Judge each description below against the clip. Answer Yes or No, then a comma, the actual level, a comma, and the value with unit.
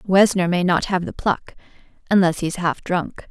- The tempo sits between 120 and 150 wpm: No, average, 200 wpm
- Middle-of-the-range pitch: Yes, medium, 180 Hz